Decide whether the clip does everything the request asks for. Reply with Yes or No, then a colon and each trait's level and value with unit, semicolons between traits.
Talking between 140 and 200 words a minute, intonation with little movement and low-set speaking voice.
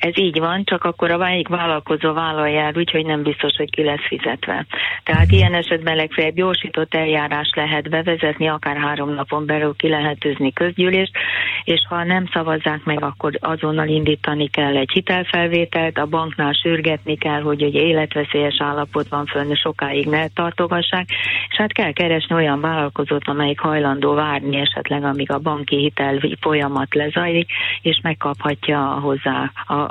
No: average, 150 wpm; narrow, 2.2 semitones; medium, 155 Hz